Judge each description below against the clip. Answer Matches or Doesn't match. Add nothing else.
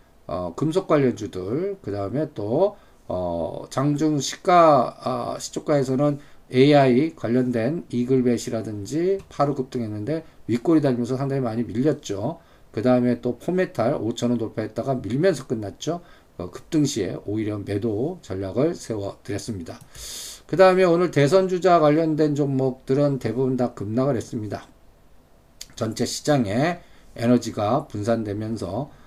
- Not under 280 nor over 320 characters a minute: Matches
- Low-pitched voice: Matches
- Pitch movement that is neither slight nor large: Matches